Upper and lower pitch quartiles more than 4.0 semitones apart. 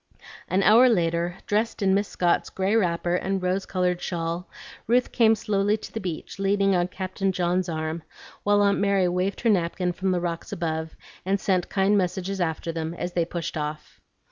No: narrow, 2.5 semitones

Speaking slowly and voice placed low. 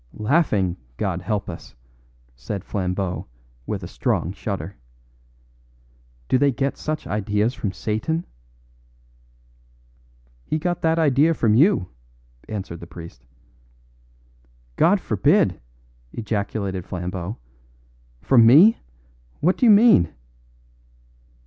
Yes: slow, 100 wpm; low, 105 Hz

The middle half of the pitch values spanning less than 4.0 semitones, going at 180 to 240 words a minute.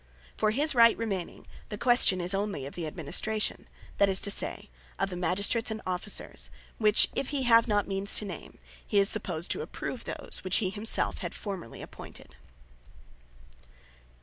No: average, 3.1 semitones; average, 170 wpm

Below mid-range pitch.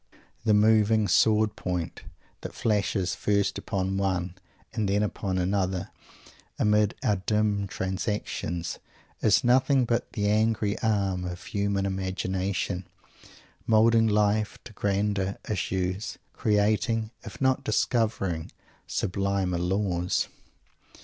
Yes: low, 100 Hz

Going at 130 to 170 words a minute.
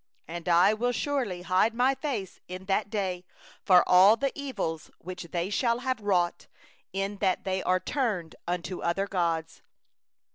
Yes: average, 155 wpm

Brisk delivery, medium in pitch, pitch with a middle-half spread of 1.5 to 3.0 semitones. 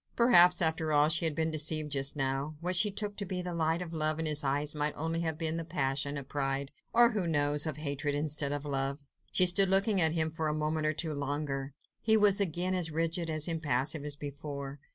Yes: fast, 230 wpm; medium, 155 Hz; average, 2.7 semitones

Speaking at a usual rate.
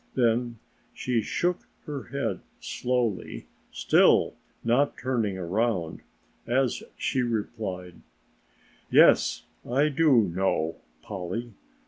No: slow, 90 wpm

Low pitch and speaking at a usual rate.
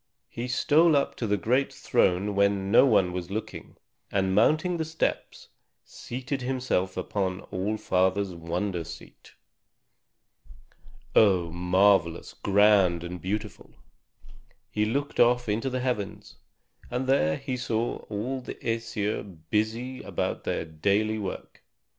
No: low, 105 Hz; slow, 125 wpm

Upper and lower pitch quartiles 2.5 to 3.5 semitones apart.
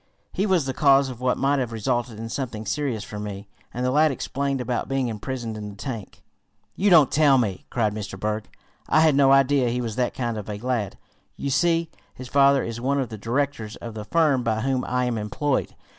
No: average, 3.9 semitones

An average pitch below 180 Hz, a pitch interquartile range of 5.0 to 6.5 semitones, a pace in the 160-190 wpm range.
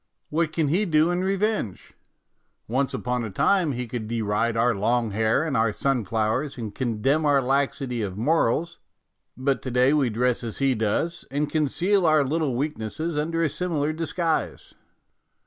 Yes: low, 135 Hz; wide, 5.4 semitones; average, 165 wpm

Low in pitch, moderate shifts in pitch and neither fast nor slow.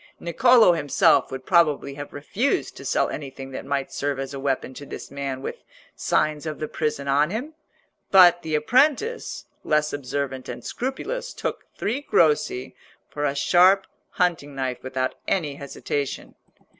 No: medium, 150 Hz; average, 4.8 semitones; average, 155 wpm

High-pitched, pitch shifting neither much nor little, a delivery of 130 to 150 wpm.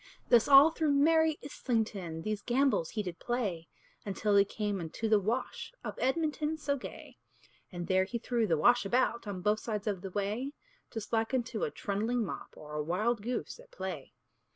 No: high, 225 Hz; average, 4.7 semitones; average, 185 wpm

